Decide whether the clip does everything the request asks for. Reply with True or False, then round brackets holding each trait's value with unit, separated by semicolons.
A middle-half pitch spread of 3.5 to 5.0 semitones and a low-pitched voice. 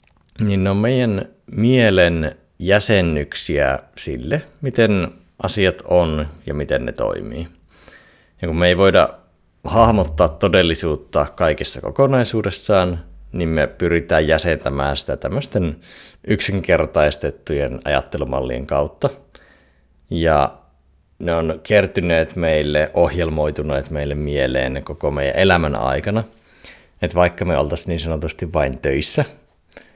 True (4.2 semitones; 85 Hz)